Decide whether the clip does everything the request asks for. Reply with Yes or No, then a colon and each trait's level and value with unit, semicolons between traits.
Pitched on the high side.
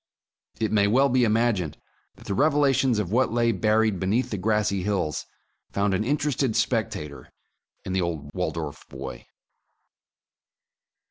No: low, 105 Hz